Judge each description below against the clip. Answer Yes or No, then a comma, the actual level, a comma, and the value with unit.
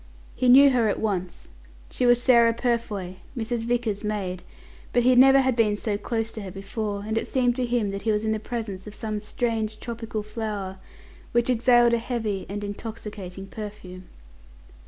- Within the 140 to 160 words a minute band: No, average, 180 wpm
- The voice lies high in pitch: Yes, high, 220 Hz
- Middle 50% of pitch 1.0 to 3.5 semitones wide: Yes, average, 2.7 semitones